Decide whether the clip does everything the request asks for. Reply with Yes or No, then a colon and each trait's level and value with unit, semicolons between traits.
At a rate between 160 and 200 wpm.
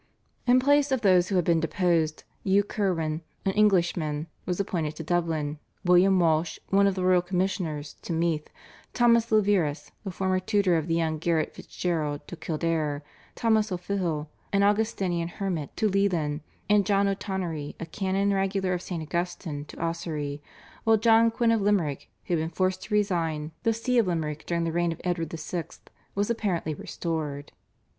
Yes: average, 170 wpm